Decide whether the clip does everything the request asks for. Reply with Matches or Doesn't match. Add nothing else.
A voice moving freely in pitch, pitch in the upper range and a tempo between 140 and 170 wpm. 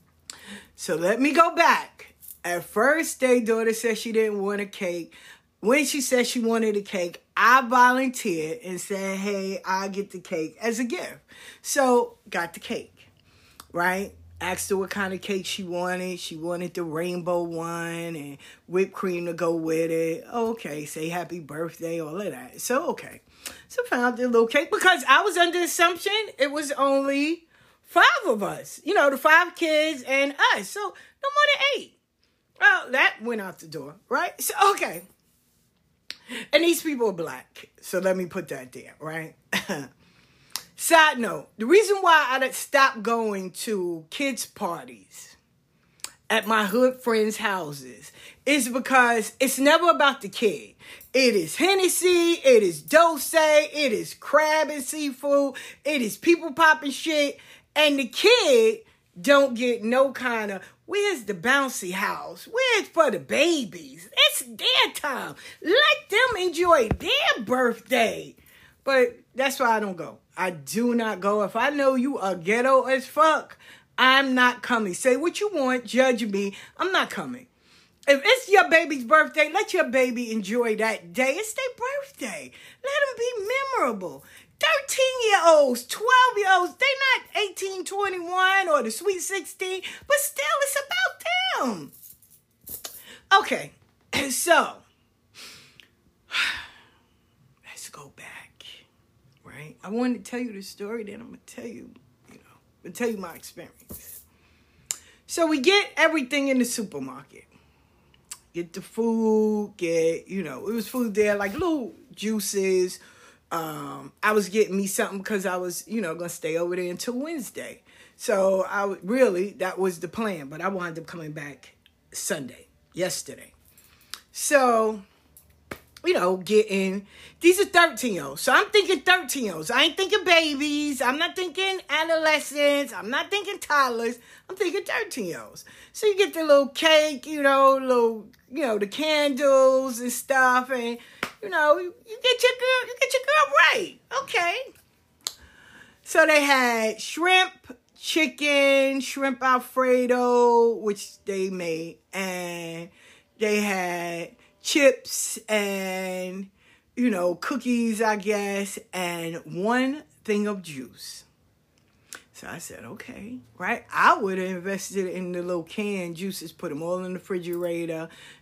Matches